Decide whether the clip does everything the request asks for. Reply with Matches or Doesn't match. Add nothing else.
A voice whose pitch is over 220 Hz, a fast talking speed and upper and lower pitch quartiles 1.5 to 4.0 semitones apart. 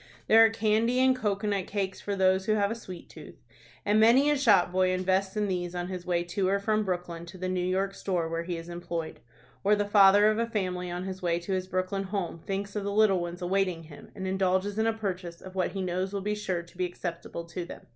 Doesn't match